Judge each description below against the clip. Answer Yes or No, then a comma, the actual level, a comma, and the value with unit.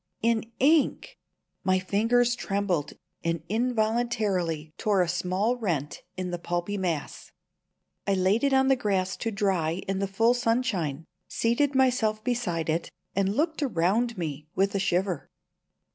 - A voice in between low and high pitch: No, high, 200 Hz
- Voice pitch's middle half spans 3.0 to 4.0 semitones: No, average, 4.9 semitones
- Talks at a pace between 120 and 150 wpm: Yes, average, 145 wpm